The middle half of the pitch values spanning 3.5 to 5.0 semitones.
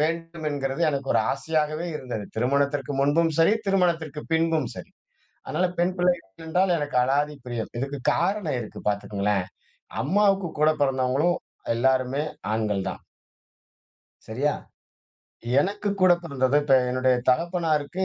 Yes: average, 4.4 semitones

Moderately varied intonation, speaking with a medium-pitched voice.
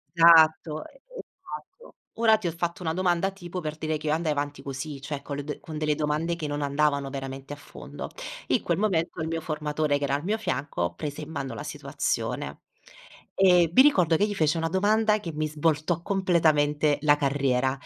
Yes: average, 3.0 semitones; medium, 155 Hz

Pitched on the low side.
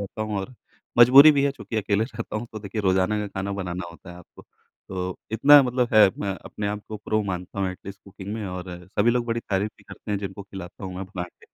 Yes: low, 100 Hz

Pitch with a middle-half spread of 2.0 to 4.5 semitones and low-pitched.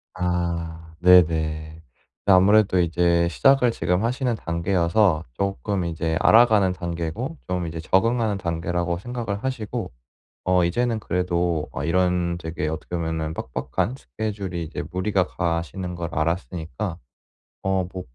Yes: average, 3.1 semitones; very low, 90 Hz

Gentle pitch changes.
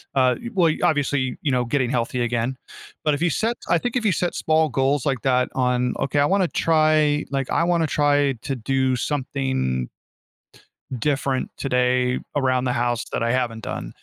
No: average, 3.1 semitones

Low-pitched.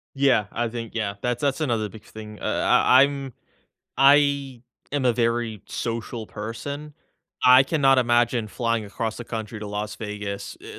Yes: low, 120 Hz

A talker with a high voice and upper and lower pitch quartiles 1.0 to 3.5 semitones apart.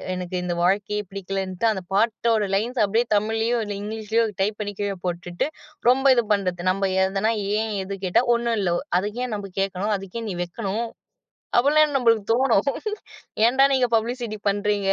Yes: high, 210 Hz; average, 3.0 semitones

